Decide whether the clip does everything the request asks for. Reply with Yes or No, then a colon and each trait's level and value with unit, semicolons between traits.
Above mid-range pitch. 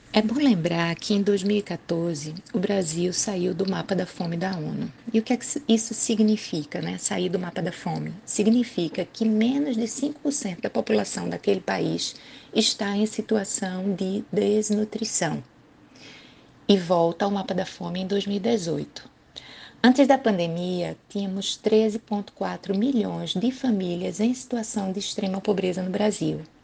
Yes: high, 200 Hz